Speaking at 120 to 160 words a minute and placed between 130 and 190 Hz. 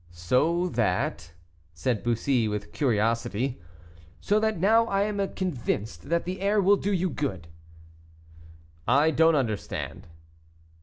Yes: slow, 135 wpm; medium, 140 Hz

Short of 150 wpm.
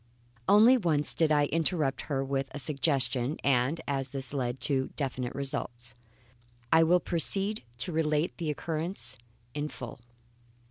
Yes: average, 140 wpm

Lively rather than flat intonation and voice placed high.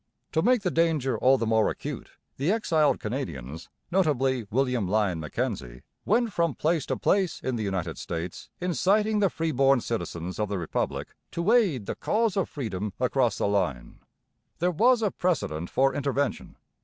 No: wide, 9.0 semitones; low, 135 Hz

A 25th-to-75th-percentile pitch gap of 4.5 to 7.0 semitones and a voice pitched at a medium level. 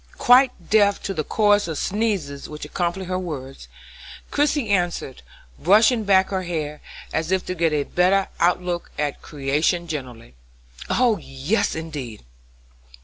Yes: average, 5.1 semitones; medium, 175 Hz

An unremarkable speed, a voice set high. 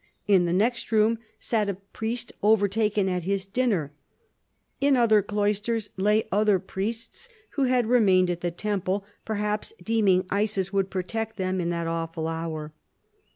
Yes: average, 150 wpm; high, 205 Hz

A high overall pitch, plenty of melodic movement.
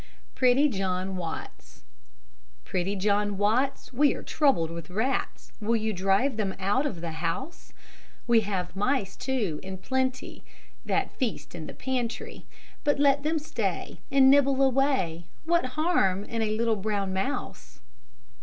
Yes: high, 220 Hz; wide, 5.9 semitones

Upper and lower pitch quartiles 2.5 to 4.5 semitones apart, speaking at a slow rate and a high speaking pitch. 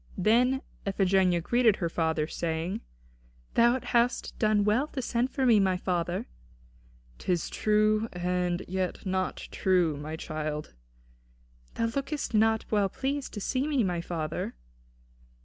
No: average, 5.1 semitones; slow, 130 wpm; high, 195 Hz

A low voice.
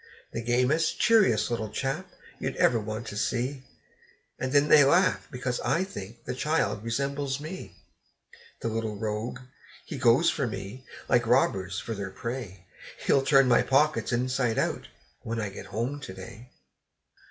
Yes: low, 125 Hz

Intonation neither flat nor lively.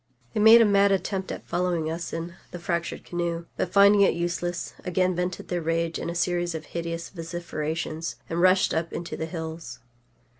No: narrow, 1.8 semitones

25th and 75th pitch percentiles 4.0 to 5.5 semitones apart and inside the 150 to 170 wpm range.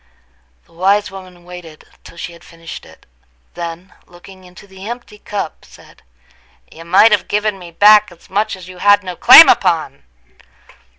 No: average, 3.1 semitones; average, 160 wpm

